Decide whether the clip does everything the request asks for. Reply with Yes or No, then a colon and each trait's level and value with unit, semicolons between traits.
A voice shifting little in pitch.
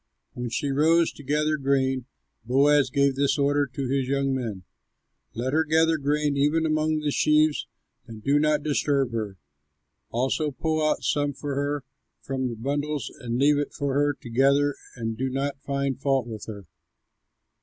Yes: narrow, 2.1 semitones